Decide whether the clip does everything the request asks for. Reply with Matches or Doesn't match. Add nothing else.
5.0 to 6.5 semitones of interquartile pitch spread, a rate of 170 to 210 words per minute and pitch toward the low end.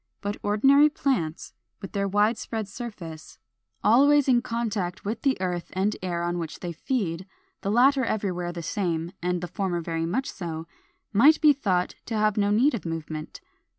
Doesn't match